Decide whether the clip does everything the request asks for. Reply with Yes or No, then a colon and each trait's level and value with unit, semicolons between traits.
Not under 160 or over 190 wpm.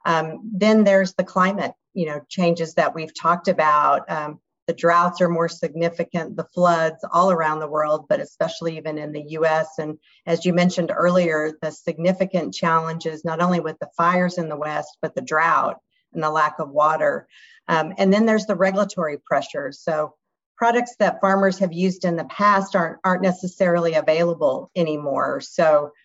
Yes: average, 175 wpm